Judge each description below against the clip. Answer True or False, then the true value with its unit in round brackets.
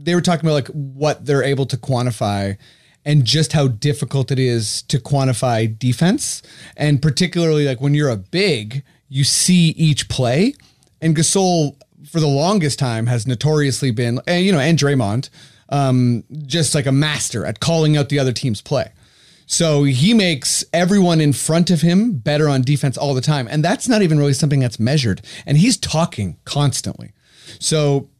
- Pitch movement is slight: False (3.7 semitones)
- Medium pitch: True (145 Hz)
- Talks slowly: False (175 wpm)